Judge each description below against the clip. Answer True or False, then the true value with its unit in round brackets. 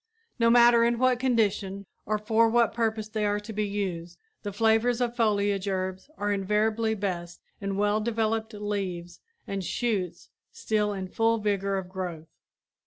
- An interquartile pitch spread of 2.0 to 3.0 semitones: True (2.5 semitones)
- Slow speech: False (160 wpm)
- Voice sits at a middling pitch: False (210 Hz)